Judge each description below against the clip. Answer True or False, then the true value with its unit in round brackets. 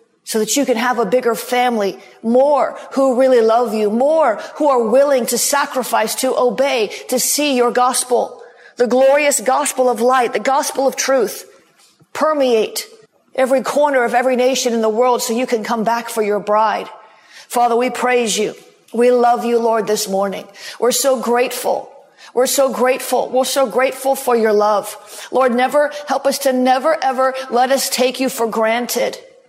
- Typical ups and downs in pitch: False (2.3 semitones)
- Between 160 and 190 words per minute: True (175 wpm)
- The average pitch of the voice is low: False (250 Hz)